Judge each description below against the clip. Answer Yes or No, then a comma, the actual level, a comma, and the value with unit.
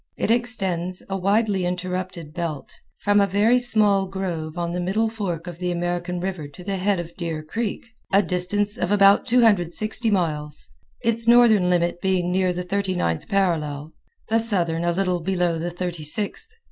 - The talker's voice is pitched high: No, medium, 180 Hz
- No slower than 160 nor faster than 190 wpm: Yes, average, 170 wpm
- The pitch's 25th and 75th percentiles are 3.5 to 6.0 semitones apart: No, average, 2.9 semitones